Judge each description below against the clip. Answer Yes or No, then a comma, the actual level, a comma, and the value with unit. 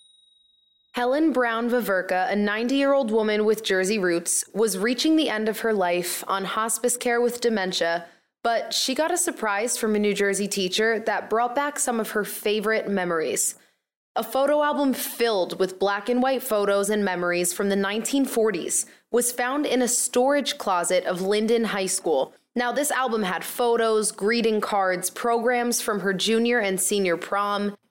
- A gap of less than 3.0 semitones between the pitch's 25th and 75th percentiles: No, average, 3.7 semitones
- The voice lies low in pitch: No, high, 220 Hz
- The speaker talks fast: No, average, 170 wpm